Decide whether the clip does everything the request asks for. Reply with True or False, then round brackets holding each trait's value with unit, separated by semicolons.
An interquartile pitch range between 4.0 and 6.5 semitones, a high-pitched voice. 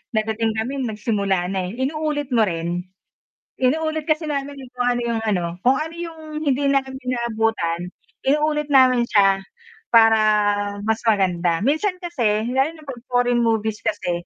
True (5.1 semitones; 240 Hz)